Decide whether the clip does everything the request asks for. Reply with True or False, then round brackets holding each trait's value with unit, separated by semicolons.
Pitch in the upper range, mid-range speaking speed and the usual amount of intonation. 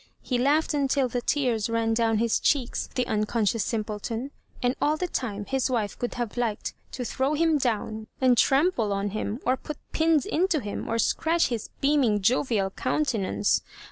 True (245 Hz; 175 wpm; 4.4 semitones)